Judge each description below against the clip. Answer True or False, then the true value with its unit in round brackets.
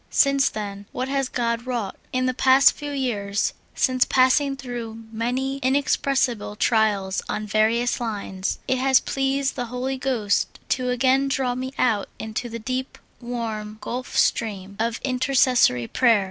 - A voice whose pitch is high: True (245 Hz)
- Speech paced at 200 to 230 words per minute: False (150 wpm)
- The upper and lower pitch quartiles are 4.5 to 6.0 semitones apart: False (3.2 semitones)